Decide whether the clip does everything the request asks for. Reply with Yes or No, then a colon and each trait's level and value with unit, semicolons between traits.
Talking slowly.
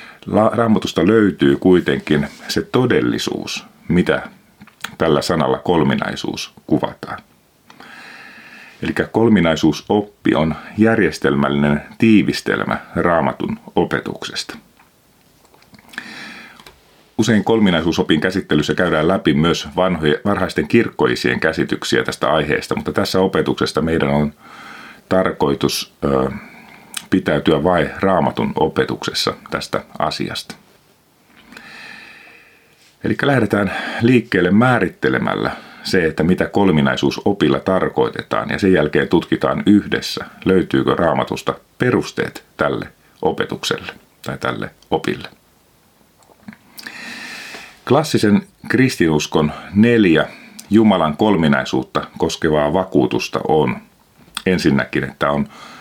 Yes: slow, 80 wpm